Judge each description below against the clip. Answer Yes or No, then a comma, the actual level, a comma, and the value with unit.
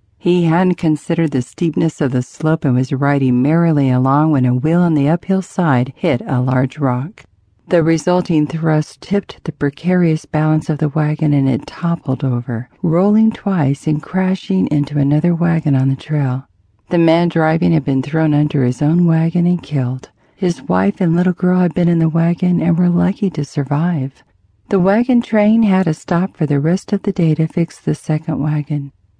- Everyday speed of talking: Yes, average, 190 wpm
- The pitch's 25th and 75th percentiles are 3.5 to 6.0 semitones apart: Yes, average, 3.9 semitones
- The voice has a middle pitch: Yes, medium, 160 Hz